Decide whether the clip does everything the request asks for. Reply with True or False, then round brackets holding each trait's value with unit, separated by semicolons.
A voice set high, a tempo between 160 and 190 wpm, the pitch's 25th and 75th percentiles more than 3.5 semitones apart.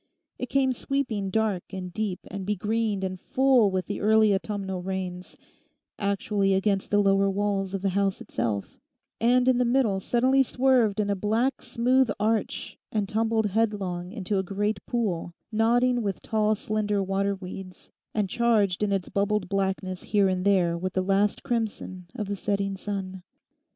False (200 Hz; 165 wpm; 2.6 semitones)